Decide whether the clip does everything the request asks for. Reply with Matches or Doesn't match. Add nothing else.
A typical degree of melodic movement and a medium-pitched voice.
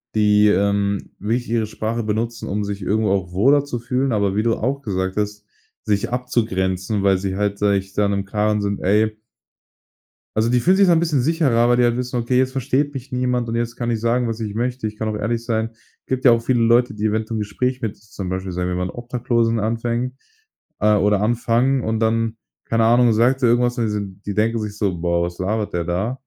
Doesn't match